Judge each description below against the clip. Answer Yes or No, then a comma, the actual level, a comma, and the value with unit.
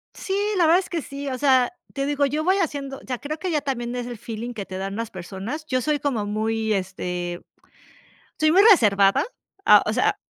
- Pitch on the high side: Yes, very high, 255 Hz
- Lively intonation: Yes, wide, 5.9 semitones